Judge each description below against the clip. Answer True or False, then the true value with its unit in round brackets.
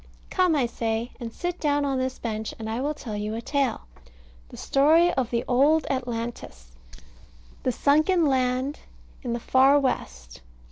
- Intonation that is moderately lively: True (3.9 semitones)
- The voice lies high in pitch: True (255 Hz)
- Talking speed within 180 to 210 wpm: False (160 wpm)